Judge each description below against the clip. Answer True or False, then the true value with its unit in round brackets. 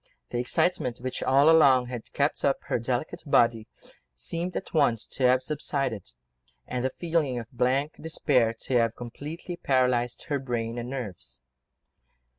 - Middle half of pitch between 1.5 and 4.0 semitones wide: True (3.1 semitones)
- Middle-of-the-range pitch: False (125 Hz)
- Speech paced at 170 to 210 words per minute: False (150 wpm)